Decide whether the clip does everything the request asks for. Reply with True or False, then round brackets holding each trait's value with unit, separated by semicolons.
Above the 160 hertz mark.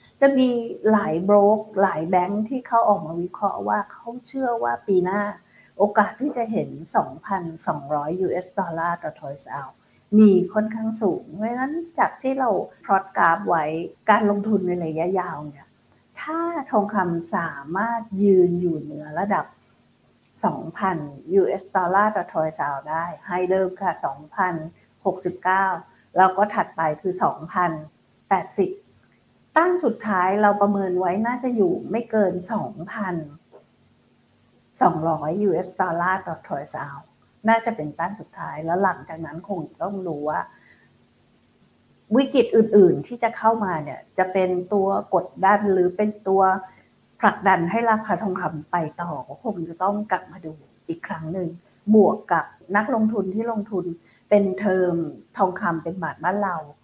True (190 Hz)